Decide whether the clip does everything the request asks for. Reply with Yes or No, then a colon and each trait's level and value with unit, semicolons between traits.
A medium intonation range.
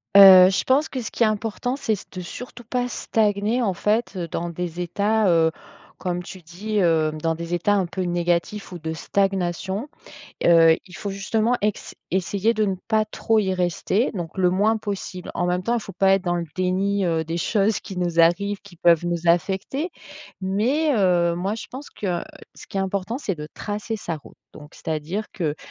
Yes: average, 3.4 semitones